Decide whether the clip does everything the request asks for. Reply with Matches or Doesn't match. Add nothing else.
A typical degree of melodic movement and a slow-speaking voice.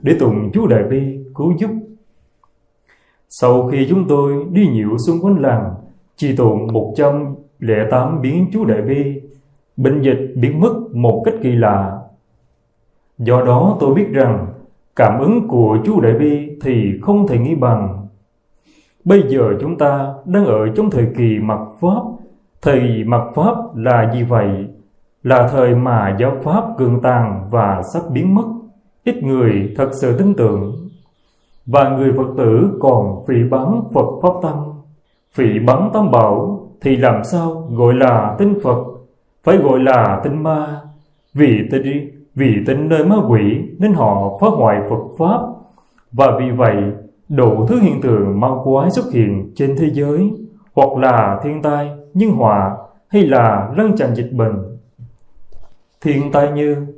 Matches